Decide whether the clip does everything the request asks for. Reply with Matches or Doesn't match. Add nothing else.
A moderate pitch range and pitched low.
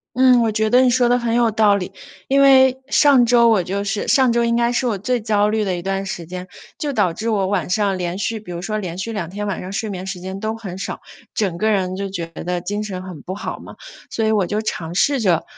Doesn't match